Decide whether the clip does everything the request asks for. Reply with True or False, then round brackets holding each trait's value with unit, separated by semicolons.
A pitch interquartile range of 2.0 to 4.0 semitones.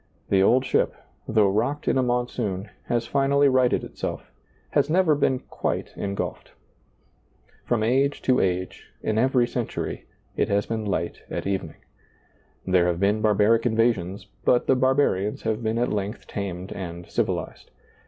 False (4.4 semitones)